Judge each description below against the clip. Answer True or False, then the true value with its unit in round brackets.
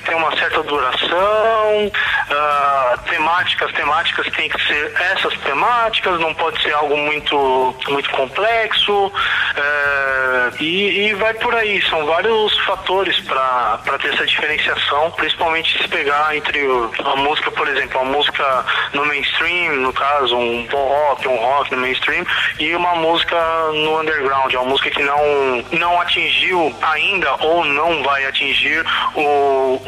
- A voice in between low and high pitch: True (150 Hz)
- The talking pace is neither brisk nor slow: True (145 wpm)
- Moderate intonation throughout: True (4.3 semitones)